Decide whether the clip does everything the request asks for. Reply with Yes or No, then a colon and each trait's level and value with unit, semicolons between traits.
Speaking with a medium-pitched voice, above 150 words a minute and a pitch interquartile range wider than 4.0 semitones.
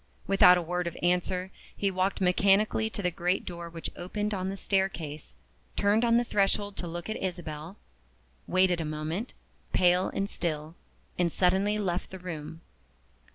No: medium, 180 Hz; average, 160 wpm; narrow, 2.5 semitones